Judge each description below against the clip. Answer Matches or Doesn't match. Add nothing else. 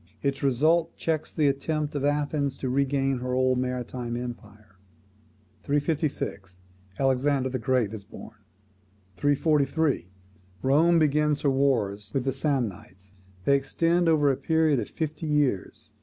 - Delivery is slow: Matches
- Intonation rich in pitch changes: Doesn't match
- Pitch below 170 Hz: Matches